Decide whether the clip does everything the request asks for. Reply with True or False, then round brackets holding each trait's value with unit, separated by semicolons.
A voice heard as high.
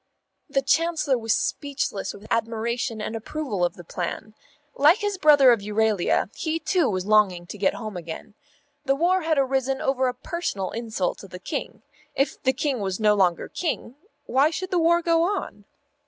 True (250 Hz)